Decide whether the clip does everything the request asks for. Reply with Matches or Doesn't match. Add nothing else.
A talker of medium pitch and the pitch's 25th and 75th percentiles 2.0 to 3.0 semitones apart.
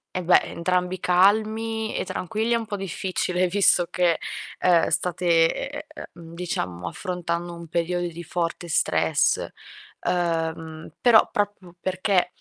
Matches